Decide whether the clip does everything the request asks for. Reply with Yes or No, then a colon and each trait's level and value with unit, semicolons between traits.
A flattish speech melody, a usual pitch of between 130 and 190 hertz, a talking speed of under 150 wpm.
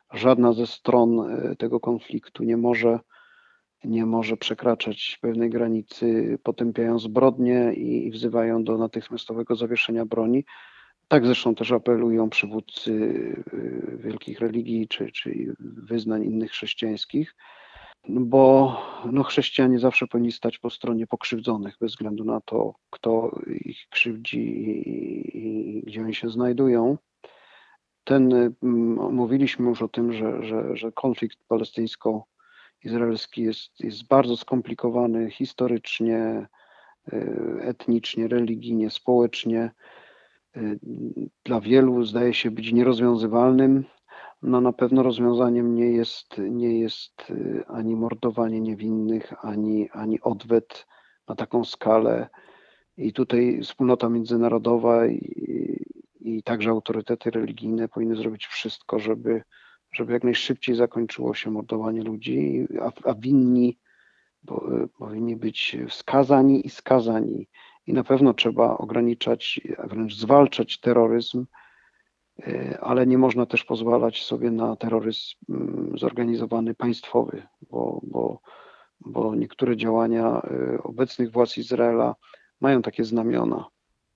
No: narrow, 1.4 semitones; low, 115 Hz; slow, 110 wpm